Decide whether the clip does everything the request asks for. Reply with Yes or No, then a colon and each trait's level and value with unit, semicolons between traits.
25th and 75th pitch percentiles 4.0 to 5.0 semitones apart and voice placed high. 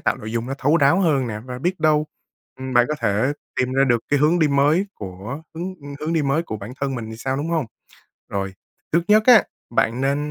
No: average, 4.6 semitones; medium, 140 Hz